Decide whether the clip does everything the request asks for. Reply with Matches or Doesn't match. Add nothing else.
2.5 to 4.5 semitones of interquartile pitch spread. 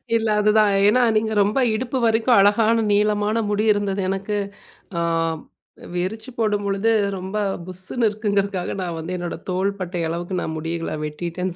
Matches